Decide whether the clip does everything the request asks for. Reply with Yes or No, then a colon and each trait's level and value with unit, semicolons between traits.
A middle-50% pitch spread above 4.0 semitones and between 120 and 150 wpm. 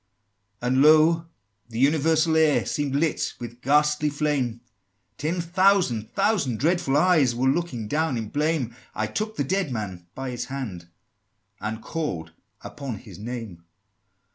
Yes: average, 5.2 semitones; average, 140 wpm